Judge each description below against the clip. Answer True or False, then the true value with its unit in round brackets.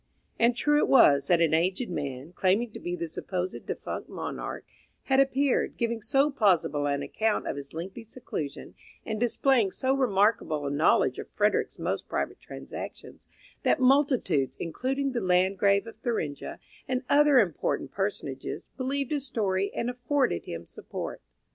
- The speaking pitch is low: False (210 Hz)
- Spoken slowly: False (155 wpm)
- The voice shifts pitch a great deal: True (7.3 semitones)